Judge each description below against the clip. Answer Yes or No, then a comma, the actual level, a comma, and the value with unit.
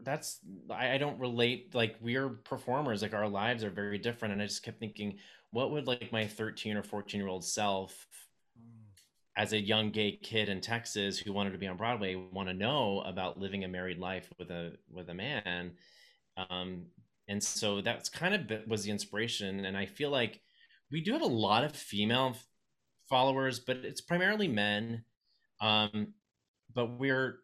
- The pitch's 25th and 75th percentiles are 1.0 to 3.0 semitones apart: No, average, 3.4 semitones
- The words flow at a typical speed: Yes, average, 185 wpm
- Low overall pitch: Yes, low, 105 Hz